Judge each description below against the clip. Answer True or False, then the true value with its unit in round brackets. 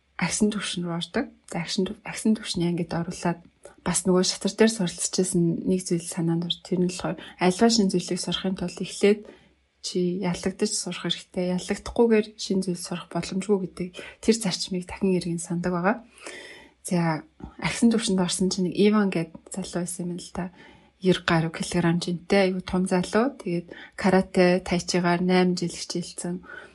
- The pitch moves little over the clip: True (2.0 semitones)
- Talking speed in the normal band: True (160 wpm)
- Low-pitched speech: False (185 Hz)